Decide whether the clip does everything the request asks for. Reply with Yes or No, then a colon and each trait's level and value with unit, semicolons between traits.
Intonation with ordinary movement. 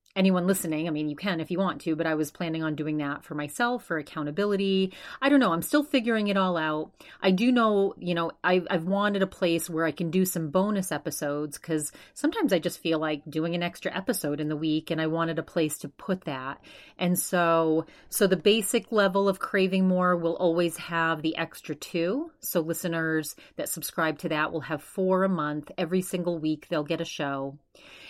Yes: average, 3.3 semitones